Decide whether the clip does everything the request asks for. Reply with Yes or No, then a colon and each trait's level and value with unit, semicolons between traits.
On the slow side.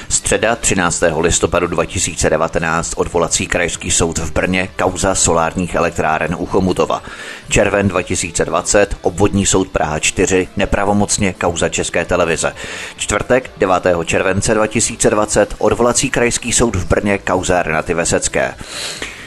Yes: slow, 110 wpm